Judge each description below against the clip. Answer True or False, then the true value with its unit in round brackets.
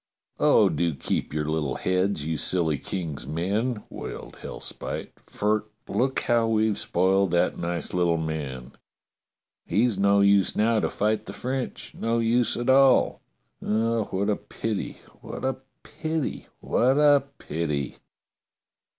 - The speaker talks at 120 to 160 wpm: True (140 wpm)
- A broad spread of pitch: True (5.8 semitones)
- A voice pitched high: False (100 Hz)